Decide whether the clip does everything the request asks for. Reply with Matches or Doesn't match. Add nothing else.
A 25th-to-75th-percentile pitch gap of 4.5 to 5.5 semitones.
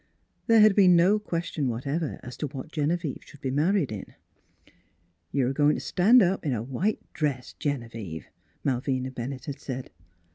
Matches